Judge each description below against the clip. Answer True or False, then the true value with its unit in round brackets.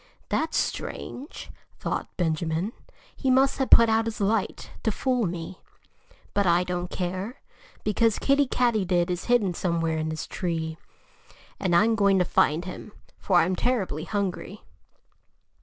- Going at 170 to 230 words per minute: False (140 wpm)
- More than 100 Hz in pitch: True (190 Hz)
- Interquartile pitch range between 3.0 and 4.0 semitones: False (4.5 semitones)